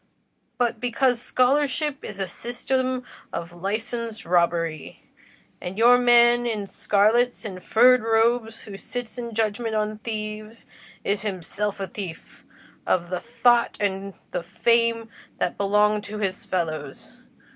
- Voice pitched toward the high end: Yes, high, 215 Hz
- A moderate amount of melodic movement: Yes, average, 3.5 semitones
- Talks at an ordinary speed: No, slow, 130 wpm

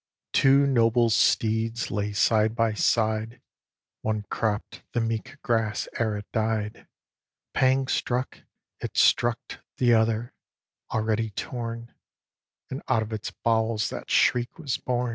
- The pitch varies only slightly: Yes, narrow, 1.7 semitones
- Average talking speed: No, slow, 125 wpm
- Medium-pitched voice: No, low, 115 Hz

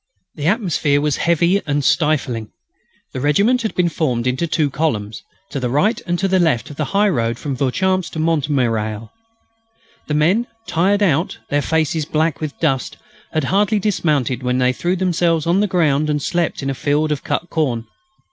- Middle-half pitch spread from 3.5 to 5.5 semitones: Yes, average, 4.3 semitones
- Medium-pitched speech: Yes, medium, 155 Hz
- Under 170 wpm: No, average, 180 wpm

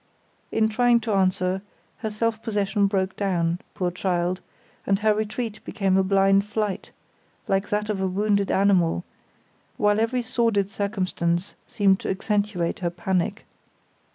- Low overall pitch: No, high, 200 Hz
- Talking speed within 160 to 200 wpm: No, average, 140 wpm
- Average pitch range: No, narrow, 2.3 semitones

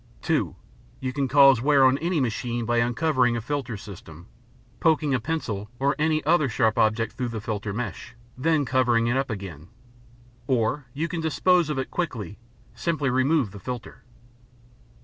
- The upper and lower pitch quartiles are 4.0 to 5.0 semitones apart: Yes, average, 4.5 semitones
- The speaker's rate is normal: Yes, average, 170 wpm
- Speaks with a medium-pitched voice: No, low, 130 Hz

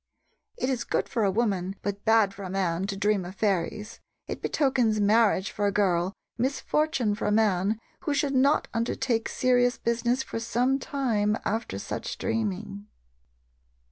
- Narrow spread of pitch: No, average, 3.6 semitones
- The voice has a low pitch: No, high, 220 Hz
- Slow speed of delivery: No, average, 160 wpm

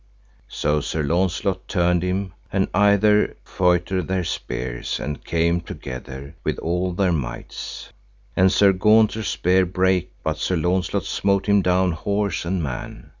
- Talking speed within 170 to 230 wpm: No, average, 140 wpm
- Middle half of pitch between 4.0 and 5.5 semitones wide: No, average, 2.7 semitones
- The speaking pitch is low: Yes, very low, 90 Hz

